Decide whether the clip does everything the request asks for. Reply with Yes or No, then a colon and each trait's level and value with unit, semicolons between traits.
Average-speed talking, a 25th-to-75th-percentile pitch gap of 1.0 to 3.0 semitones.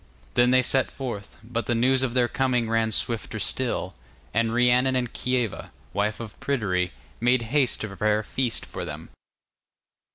Yes: average, 165 wpm; narrow, 2.5 semitones